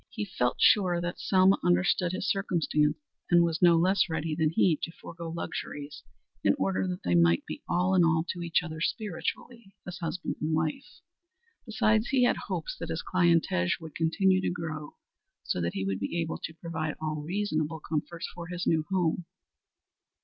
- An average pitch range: Yes, average, 3.0 semitones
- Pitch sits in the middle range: Yes, medium, 170 Hz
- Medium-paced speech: Yes, average, 180 wpm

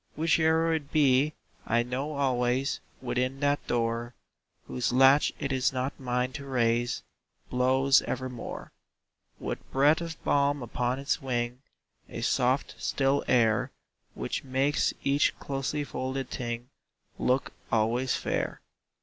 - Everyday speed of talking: No, slow, 125 wpm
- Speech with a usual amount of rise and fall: No, narrow, 2.3 semitones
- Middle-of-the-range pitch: No, low, 130 Hz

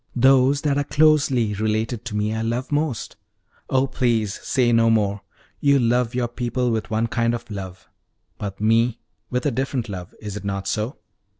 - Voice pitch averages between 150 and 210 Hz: No, low, 115 Hz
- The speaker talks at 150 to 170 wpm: No, average, 180 wpm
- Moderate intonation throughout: Yes, average, 3.2 semitones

